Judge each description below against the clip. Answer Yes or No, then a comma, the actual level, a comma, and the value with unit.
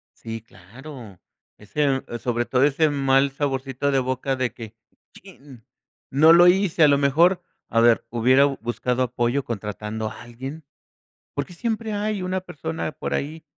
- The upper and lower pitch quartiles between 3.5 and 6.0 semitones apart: Yes, average, 4.7 semitones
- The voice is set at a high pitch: No, low, 135 Hz